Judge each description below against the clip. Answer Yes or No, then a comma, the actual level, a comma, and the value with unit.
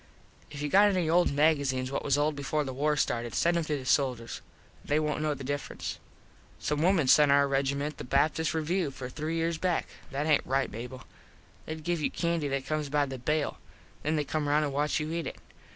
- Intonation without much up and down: Yes, narrow, 2.3 semitones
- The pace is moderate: No, fast, 215 wpm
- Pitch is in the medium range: Yes, medium, 150 Hz